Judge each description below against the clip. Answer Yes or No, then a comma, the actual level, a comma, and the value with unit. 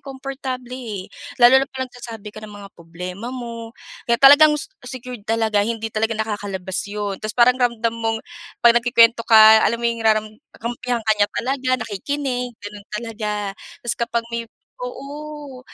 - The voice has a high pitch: Yes, high, 230 Hz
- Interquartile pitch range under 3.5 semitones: Yes, average, 2.8 semitones